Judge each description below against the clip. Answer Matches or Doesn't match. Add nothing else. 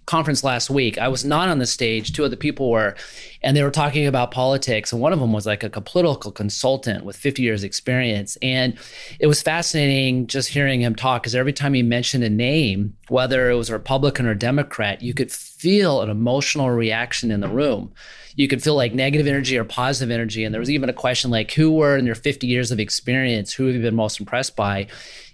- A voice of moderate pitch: Doesn't match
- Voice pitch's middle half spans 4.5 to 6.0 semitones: Doesn't match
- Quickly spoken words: Matches